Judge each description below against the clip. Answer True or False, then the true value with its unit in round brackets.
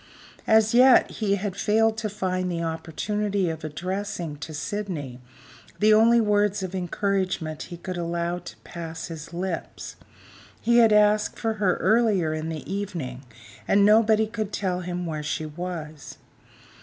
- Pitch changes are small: False (4.2 semitones)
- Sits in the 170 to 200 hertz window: True (185 Hz)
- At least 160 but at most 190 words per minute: False (150 wpm)